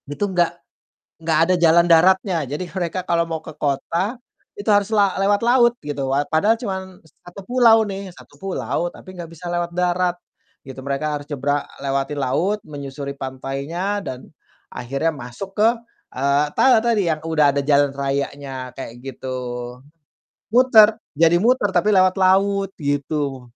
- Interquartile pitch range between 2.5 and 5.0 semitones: No, wide, 5.6 semitones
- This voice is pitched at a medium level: Yes, medium, 165 Hz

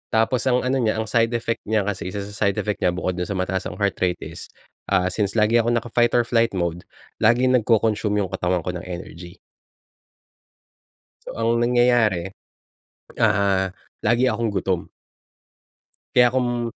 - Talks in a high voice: No, low, 105 Hz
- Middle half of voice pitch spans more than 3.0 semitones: Yes, average, 4.1 semitones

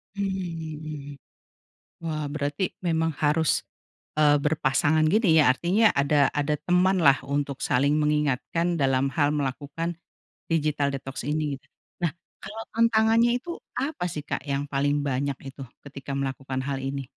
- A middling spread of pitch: Yes, average, 3.3 semitones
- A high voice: No, medium, 150 Hz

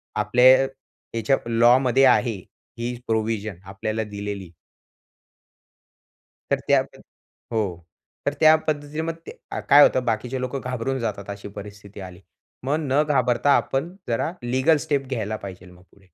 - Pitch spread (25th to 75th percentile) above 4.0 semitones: Yes, average, 4.6 semitones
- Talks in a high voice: No, low, 120 Hz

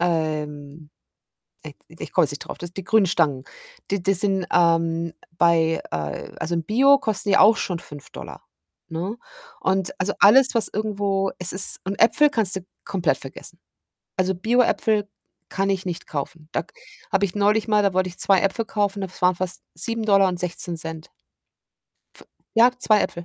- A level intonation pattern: No, average, 3.6 semitones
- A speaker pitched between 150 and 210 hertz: Yes, high, 190 Hz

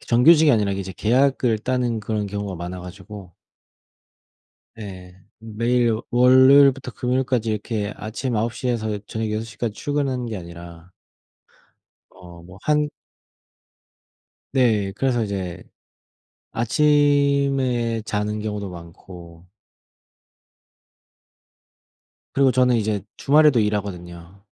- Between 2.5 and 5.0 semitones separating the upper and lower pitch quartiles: Yes, average, 4.4 semitones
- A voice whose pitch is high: No, low, 110 Hz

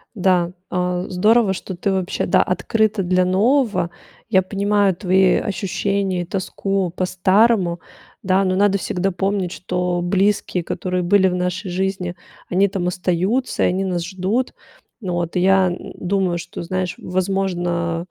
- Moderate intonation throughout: No, narrow, 1.7 semitones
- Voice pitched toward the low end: No, medium, 185 Hz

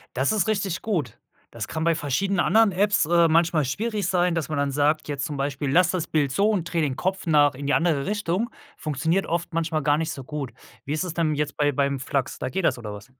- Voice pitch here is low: No, medium, 160 Hz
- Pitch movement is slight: No, average, 4.1 semitones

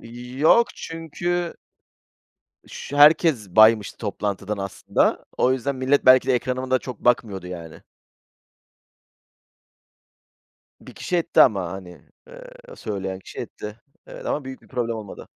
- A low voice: Yes, low, 125 Hz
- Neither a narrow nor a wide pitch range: No, wide, 5.7 semitones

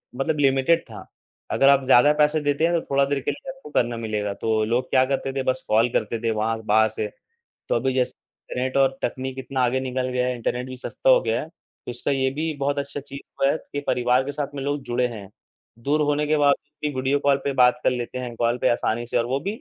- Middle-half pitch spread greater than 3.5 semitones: No, average, 2.7 semitones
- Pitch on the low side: Yes, low, 130 Hz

